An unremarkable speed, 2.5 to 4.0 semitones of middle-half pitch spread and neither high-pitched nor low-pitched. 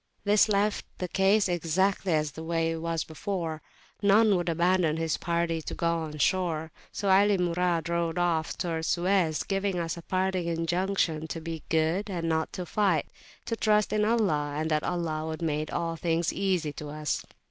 Yes: average, 170 wpm; average, 3.0 semitones; medium, 170 Hz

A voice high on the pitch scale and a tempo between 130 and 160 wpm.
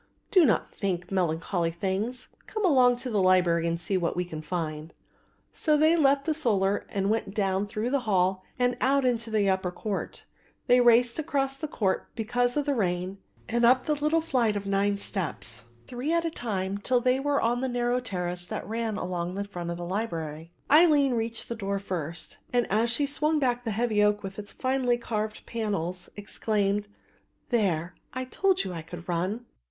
No: high, 215 Hz; average, 190 wpm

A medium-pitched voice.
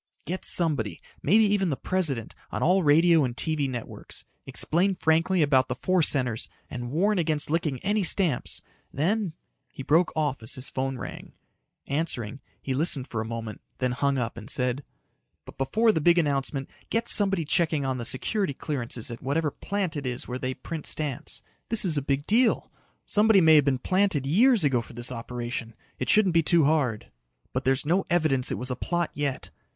Yes: medium, 145 Hz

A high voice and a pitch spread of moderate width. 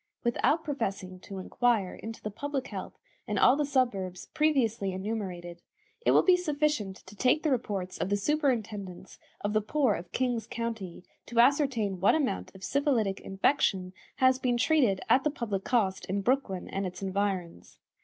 No: high, 220 Hz; wide, 5.7 semitones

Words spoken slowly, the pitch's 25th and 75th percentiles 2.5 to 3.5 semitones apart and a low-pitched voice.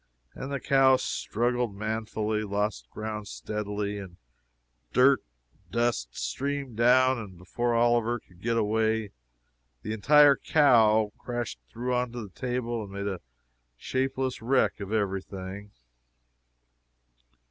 Yes: slow, 125 wpm; average, 3.2 semitones; low, 110 Hz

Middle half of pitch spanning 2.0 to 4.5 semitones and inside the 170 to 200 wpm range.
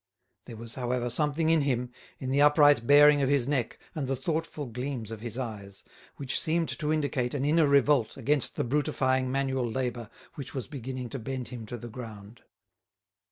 Yes: average, 3.1 semitones; average, 185 wpm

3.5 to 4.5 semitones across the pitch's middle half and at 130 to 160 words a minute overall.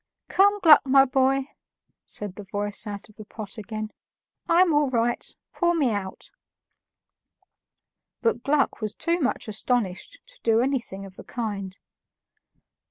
No: average, 5.2 semitones; average, 140 wpm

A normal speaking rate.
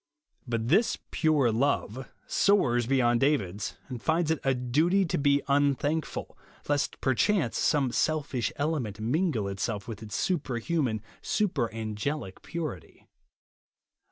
No: slow, 125 wpm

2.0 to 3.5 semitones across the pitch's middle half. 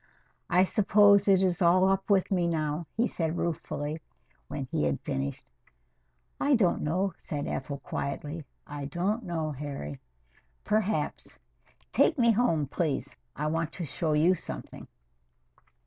No: average, 4.6 semitones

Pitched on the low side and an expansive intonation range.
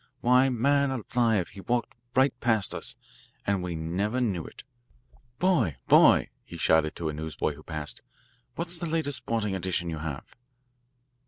Yes: low, 105 Hz; wide, 7.8 semitones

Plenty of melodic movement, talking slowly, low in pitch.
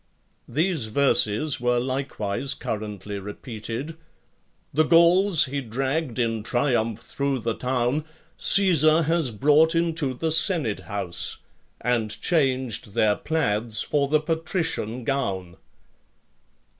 Yes: wide, 5.9 semitones; slow, 105 wpm; low, 130 Hz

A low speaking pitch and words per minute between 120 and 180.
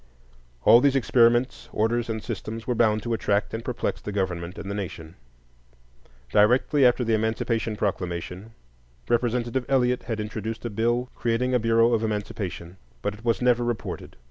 Yes: low, 115 Hz; average, 160 wpm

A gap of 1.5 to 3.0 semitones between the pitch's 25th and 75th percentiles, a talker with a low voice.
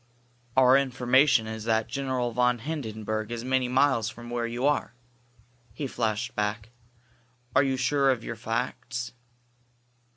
Yes: narrow, 2.6 semitones; low, 125 Hz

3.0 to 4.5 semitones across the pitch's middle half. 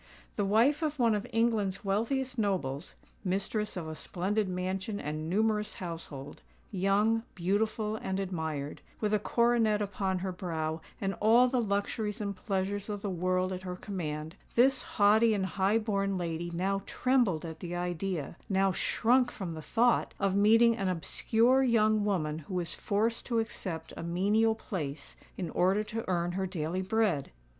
Yes: average, 3.6 semitones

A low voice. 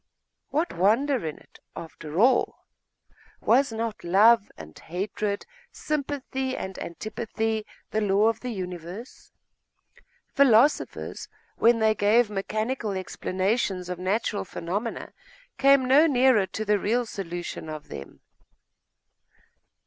No: high, 215 Hz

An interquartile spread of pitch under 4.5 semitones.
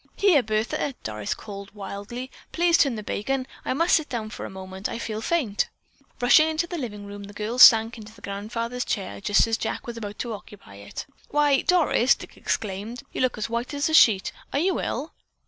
No: average, 4.9 semitones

